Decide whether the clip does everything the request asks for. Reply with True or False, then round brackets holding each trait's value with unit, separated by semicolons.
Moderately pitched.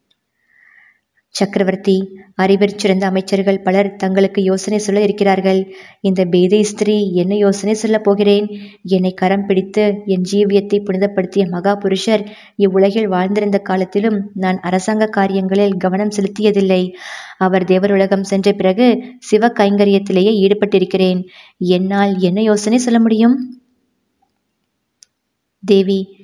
False (200 Hz)